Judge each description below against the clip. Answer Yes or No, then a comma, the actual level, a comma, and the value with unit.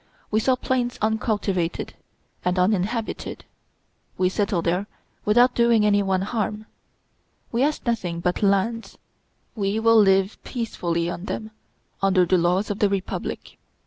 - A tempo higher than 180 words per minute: No, slow, 135 wpm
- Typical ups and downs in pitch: Yes, average, 3.5 semitones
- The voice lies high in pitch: Yes, high, 205 Hz